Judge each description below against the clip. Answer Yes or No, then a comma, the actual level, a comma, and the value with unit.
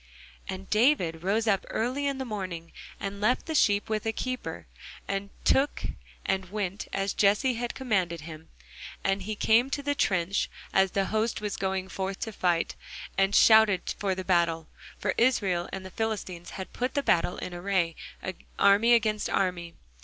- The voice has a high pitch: Yes, high, 200 Hz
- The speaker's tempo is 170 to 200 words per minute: Yes, average, 175 wpm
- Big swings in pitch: No, average, 3.2 semitones